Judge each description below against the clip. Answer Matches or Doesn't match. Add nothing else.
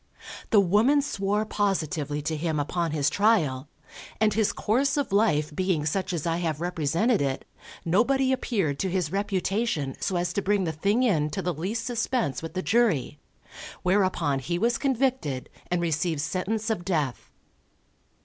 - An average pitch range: Doesn't match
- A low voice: Doesn't match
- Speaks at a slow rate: Doesn't match